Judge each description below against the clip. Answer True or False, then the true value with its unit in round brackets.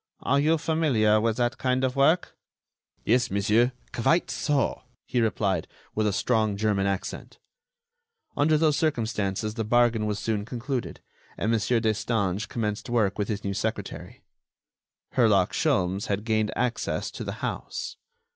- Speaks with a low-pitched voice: True (115 Hz)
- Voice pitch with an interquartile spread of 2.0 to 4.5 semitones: True (3.4 semitones)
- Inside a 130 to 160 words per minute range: True (145 wpm)